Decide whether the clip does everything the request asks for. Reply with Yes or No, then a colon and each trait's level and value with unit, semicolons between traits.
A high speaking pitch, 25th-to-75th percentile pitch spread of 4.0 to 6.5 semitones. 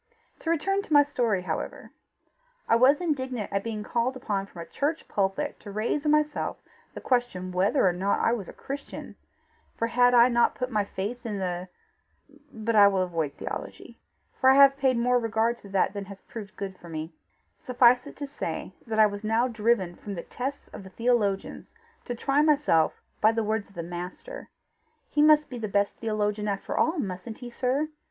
Yes: high, 225 Hz; average, 4.6 semitones